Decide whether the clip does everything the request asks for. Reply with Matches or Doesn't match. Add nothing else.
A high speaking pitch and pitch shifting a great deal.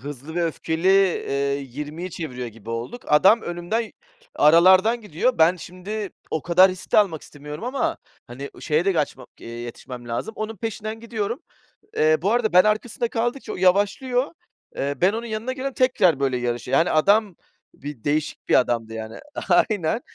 Doesn't match